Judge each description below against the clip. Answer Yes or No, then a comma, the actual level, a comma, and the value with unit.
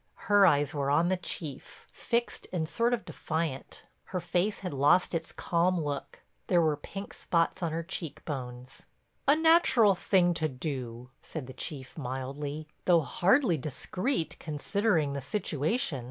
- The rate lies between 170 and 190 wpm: No, average, 155 wpm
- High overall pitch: No, medium, 160 Hz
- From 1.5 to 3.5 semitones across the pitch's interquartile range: No, average, 4.8 semitones